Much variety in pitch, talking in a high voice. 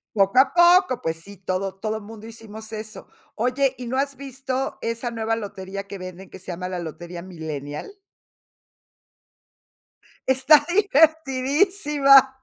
Yes: wide, 6.2 semitones; high, 225 Hz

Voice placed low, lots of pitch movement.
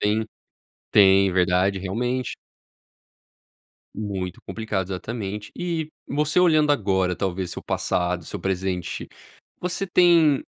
Yes: low, 100 Hz; wide, 7.6 semitones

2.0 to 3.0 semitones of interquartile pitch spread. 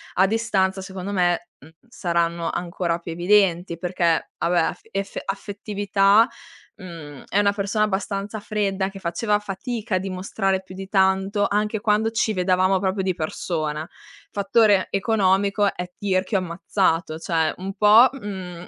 Yes: narrow, 2.5 semitones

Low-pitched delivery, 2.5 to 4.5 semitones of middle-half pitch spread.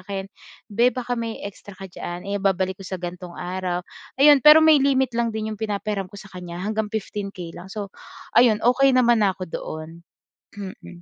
No: high, 200 Hz; average, 4.0 semitones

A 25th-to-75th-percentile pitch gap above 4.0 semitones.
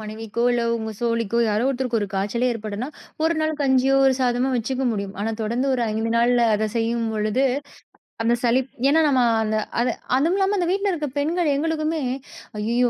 No: average, 3.7 semitones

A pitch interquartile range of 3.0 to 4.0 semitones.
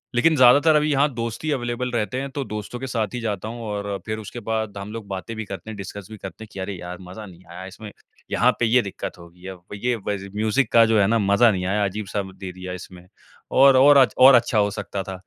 Yes: average, 3.7 semitones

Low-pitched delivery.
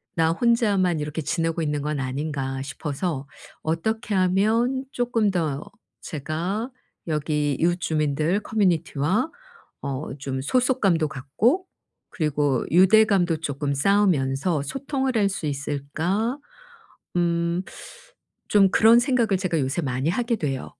No: medium, 170 Hz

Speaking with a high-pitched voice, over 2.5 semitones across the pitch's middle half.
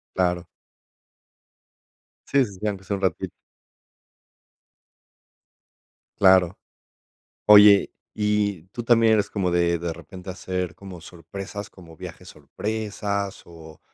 No: very low, 95 Hz; average, 2.9 semitones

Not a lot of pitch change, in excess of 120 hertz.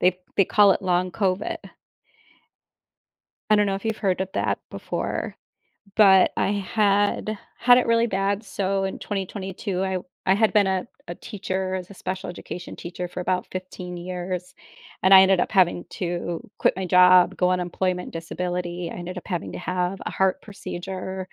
Yes: narrow, 1.5 semitones; medium, 185 Hz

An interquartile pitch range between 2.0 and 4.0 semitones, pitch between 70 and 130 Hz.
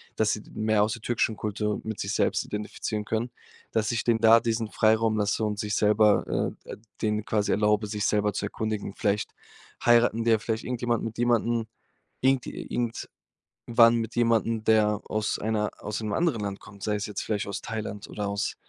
No: narrow, 1.4 semitones; low, 110 Hz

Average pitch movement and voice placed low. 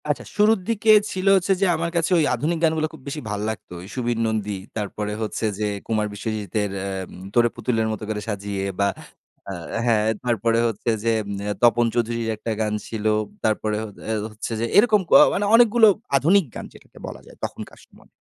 No: wide, 7.0 semitones; low, 115 Hz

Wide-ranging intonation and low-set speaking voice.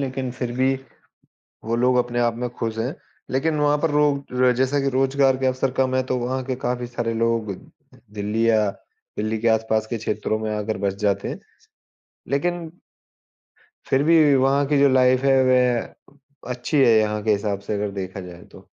No: average, 3.3 semitones; low, 125 Hz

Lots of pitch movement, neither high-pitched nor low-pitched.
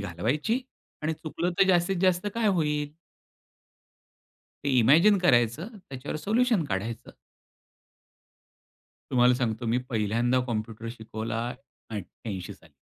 No: wide, 7.5 semitones; low, 130 Hz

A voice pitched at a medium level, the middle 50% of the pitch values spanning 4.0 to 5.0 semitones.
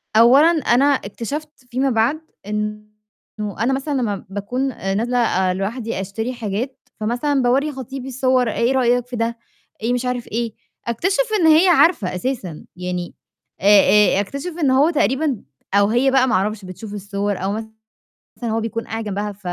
No: high, 235 Hz; average, 4.3 semitones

